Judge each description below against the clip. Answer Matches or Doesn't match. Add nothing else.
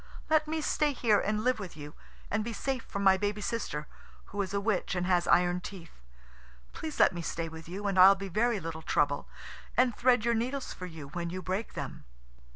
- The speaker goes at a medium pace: Doesn't match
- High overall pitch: Matches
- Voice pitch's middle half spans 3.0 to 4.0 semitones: Doesn't match